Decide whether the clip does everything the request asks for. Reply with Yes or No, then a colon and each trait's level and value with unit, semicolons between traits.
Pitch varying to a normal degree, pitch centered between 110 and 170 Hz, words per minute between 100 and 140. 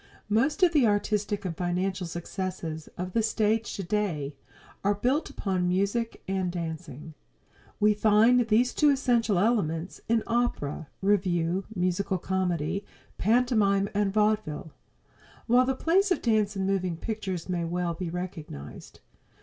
No: average, 3.9 semitones; high, 195 Hz; slow, 135 wpm